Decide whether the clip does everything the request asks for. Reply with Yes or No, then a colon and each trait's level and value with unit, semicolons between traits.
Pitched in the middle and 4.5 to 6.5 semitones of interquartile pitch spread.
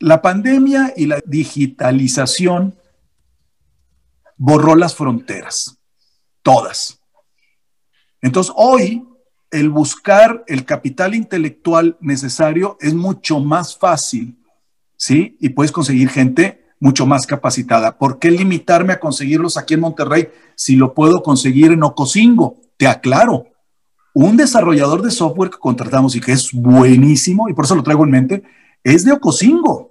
Yes: medium, 155 Hz; wide, 5.5 semitones